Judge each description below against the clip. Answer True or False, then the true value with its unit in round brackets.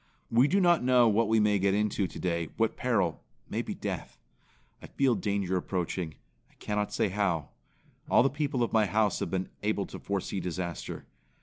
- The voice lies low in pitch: True (105 Hz)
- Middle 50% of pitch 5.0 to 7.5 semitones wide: False (3.8 semitones)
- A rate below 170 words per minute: False (180 wpm)